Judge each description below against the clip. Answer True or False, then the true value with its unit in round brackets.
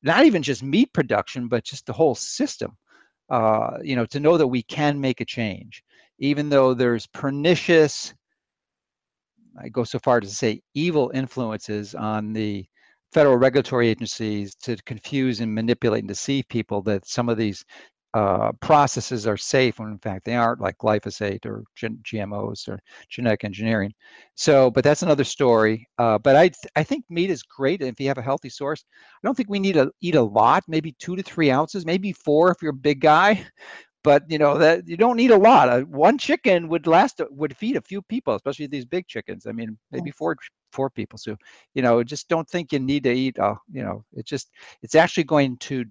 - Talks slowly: False (205 wpm)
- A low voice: True (130 Hz)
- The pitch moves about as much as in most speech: False (5.8 semitones)